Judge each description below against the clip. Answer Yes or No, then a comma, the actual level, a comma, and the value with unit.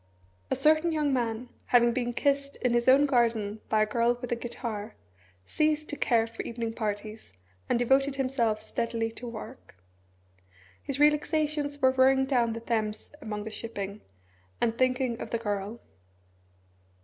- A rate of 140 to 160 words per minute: Yes, average, 155 wpm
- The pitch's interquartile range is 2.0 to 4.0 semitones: Yes, average, 3.1 semitones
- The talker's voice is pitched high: Yes, high, 240 Hz